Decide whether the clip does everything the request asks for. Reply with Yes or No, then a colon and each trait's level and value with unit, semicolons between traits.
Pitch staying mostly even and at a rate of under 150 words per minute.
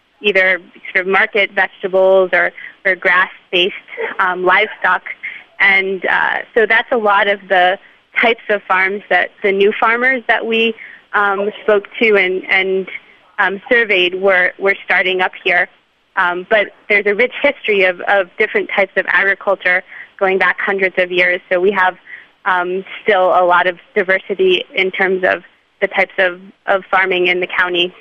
No: narrow, 2.0 semitones; average, 165 wpm